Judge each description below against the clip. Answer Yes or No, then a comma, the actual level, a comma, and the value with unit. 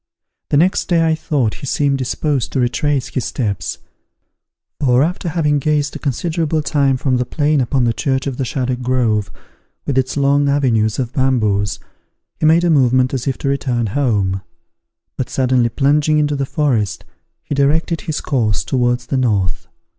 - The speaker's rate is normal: Yes, average, 170 wpm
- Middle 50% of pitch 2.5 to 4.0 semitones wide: Yes, average, 3.2 semitones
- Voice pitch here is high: No, low, 135 Hz